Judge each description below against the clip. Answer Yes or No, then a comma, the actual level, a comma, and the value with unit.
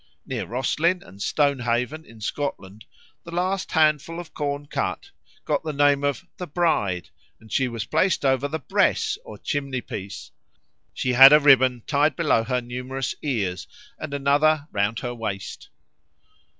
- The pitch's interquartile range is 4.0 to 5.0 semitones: Yes, average, 4.3 semitones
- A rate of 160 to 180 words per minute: No, average, 150 wpm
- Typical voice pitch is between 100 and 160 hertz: Yes, medium, 140 Hz